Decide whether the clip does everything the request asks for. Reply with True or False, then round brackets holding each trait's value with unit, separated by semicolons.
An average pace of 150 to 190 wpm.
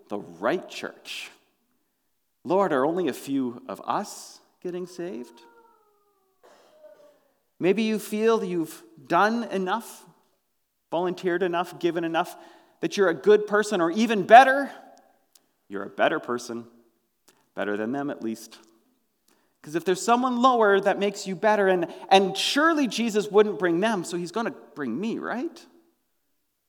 False (140 wpm)